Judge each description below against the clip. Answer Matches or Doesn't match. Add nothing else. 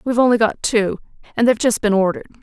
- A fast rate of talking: Matches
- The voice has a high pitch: Matches